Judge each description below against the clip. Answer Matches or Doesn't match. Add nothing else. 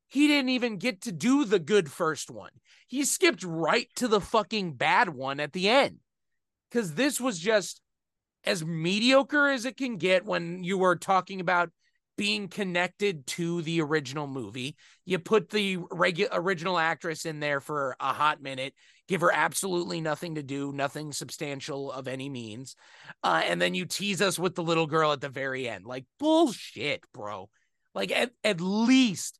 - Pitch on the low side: Doesn't match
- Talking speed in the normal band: Matches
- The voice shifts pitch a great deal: Matches